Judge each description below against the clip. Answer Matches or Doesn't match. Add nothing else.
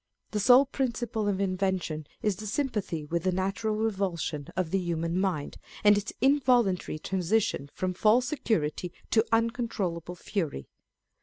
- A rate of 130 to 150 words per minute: Matches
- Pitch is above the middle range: Matches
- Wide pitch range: Doesn't match